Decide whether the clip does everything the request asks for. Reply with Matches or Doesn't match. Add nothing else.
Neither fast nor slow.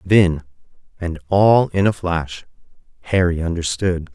Doesn't match